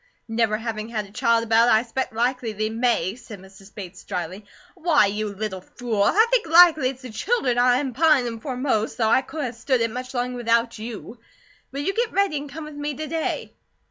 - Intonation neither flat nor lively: Yes, average, 4.4 semitones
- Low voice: No, high, 240 Hz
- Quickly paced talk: Yes, fast, 215 wpm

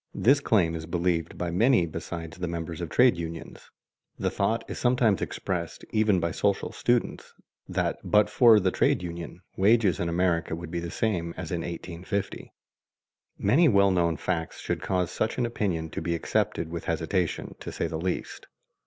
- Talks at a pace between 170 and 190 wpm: Yes, average, 175 wpm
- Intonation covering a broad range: No, average, 3.8 semitones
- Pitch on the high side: No, very low, 90 Hz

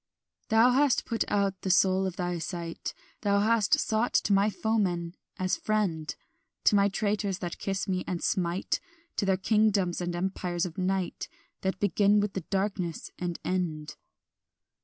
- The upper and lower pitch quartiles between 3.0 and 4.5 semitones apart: No, narrow, 2.6 semitones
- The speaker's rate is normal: Yes, average, 160 wpm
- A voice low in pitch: No, high, 190 Hz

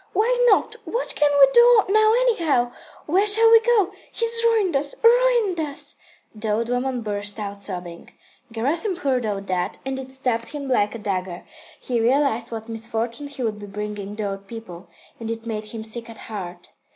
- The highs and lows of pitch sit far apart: Yes, wide, 8.7 semitones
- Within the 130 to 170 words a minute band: No, average, 185 wpm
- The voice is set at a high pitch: Yes, high, 240 Hz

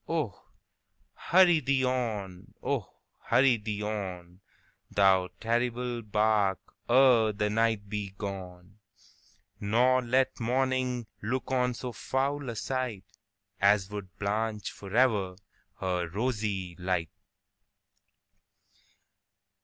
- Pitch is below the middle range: Yes, low, 110 Hz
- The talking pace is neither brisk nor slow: No, slow, 85 wpm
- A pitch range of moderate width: Yes, average, 4.2 semitones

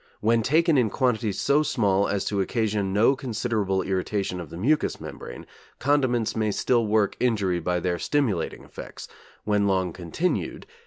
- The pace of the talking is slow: No, average, 155 wpm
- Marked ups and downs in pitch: No, average, 4.3 semitones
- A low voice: Yes, low, 105 Hz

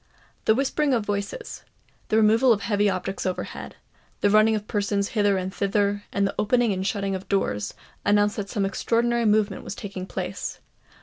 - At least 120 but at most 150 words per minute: No, average, 160 wpm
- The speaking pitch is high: Yes, high, 205 Hz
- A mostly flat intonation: Yes, narrow, 1.8 semitones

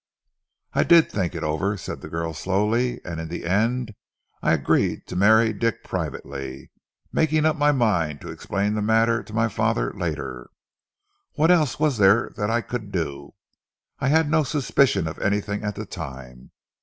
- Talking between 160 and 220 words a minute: Yes, average, 170 wpm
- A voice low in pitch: Yes, low, 105 Hz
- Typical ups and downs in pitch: No, wide, 6.2 semitones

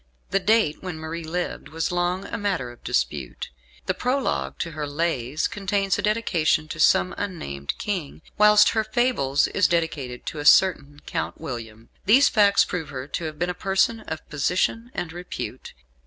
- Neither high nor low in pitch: Yes, medium, 170 Hz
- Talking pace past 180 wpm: No, average, 170 wpm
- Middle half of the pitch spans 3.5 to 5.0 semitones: No, wide, 5.5 semitones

